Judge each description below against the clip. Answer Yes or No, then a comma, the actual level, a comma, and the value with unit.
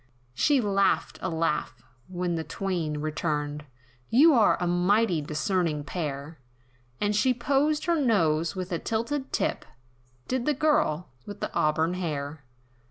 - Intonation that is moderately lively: No, wide, 6.7 semitones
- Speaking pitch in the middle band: Yes, medium, 180 Hz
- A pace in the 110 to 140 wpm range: Yes, slow, 135 wpm